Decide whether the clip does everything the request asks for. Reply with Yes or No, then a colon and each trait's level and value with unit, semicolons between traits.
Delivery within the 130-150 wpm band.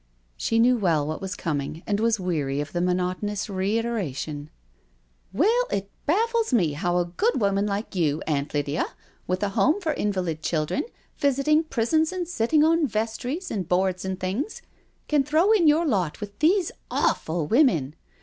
No: average, 170 wpm